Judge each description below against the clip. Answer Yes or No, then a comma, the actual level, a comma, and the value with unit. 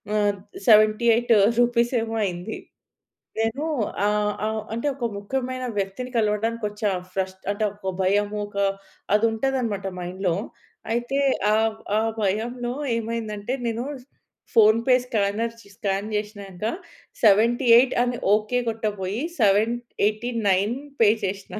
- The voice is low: No, high, 220 Hz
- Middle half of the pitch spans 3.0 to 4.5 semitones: No, narrow, 2.6 semitones